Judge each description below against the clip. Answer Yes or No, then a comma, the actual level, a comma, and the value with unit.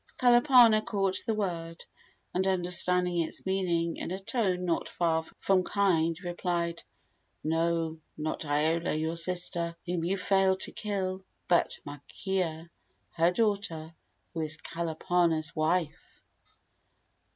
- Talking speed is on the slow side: Yes, slow, 120 wpm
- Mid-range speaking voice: Yes, medium, 175 Hz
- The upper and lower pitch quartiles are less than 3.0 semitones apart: Yes, narrow, 2.4 semitones